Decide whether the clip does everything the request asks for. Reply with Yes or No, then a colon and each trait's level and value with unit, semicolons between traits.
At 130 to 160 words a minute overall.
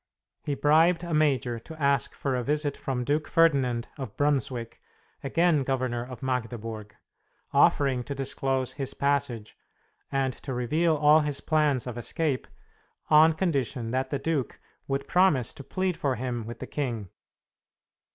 Yes: average, 150 wpm